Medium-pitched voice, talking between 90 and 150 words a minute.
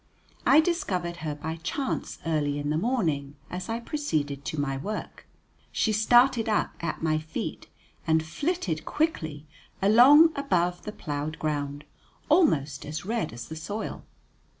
Yes: medium, 165 Hz; average, 145 wpm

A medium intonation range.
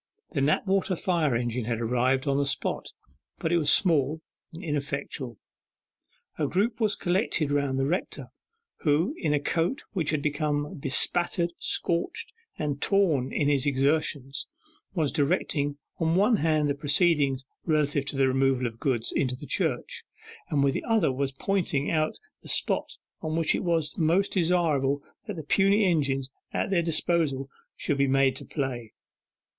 Yes: average, 3.8 semitones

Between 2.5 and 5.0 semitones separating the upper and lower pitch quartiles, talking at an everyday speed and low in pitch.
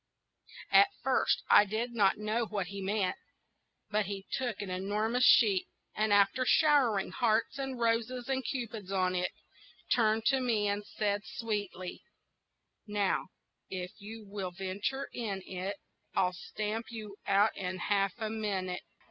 No: average, 2.9 semitones; average, 145 wpm; high, 210 Hz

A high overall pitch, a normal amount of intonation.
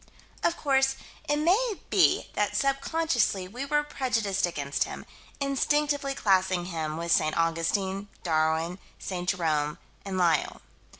No: high, 195 Hz; wide, 8.7 semitones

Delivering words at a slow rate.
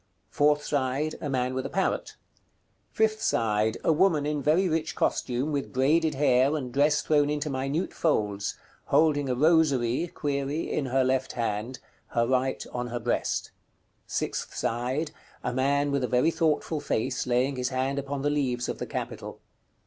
No: average, 165 wpm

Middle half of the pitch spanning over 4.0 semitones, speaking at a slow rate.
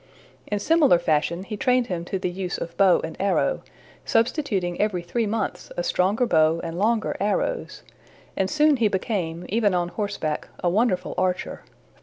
No: average, 4.4 semitones; average, 165 wpm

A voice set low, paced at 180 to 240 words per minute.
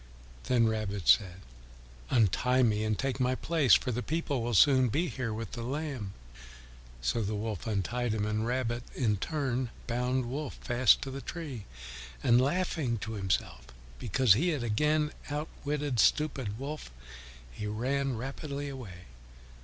No: low, 125 Hz; average, 145 wpm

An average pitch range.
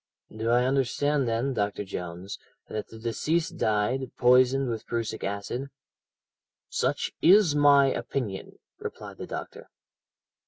Yes: average, 4.2 semitones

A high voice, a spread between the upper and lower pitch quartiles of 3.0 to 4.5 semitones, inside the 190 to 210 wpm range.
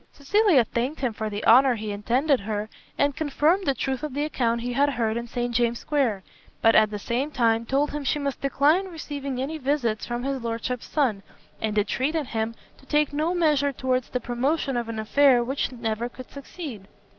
Yes: very high, 255 Hz; average, 3.8 semitones; average, 200 wpm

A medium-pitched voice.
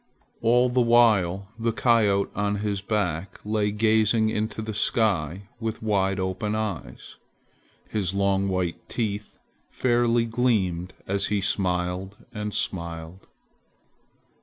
No: low, 105 Hz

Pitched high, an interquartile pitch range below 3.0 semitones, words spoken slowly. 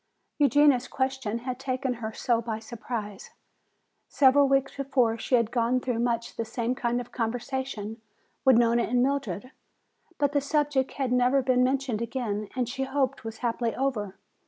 No: very high, 250 Hz; narrow, 2.6 semitones; average, 160 wpm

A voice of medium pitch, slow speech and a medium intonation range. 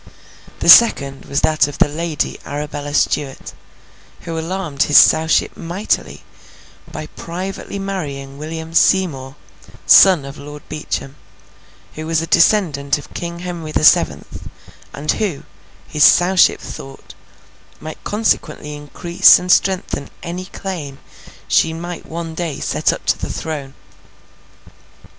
Yes: medium, 160 Hz; slow, 125 wpm; average, 3.4 semitones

